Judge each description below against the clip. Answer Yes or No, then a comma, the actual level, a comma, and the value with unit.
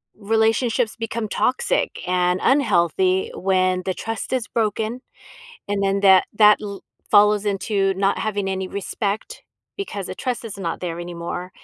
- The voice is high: Yes, high, 200 Hz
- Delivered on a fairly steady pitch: No, average, 3.0 semitones